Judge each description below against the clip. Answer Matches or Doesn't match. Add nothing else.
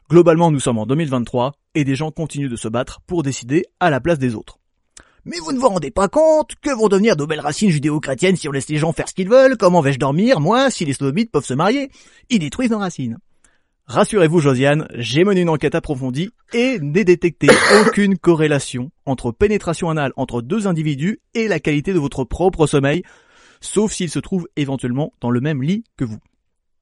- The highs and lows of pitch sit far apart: Matches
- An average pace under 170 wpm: Doesn't match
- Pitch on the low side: Doesn't match